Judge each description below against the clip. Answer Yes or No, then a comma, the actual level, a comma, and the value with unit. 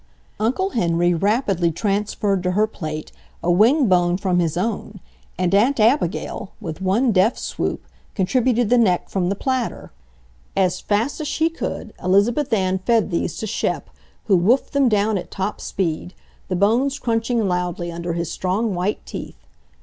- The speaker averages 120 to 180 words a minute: Yes, average, 160 wpm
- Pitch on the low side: No, high, 200 Hz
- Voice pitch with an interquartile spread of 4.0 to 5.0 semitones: Yes, average, 4.5 semitones